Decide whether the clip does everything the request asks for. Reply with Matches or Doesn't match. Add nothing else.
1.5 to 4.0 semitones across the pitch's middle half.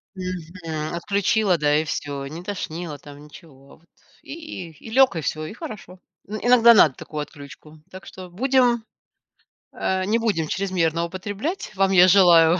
Doesn't match